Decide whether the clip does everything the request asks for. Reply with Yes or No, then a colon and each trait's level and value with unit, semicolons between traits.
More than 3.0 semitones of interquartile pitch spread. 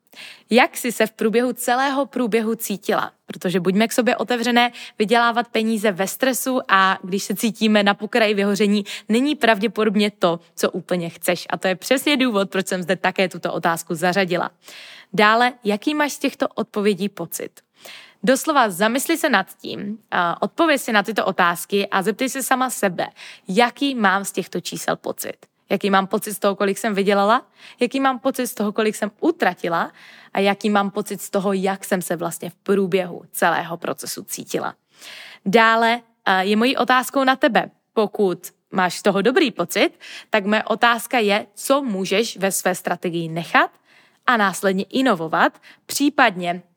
Yes: average, 4.0 semitones